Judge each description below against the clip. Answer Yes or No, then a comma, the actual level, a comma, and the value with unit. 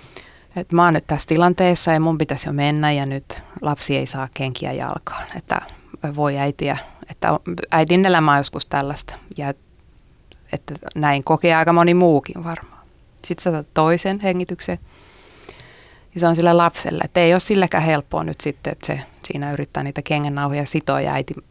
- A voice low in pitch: No, medium, 155 Hz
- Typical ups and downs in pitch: Yes, average, 3.3 semitones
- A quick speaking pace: Yes, fast, 160 wpm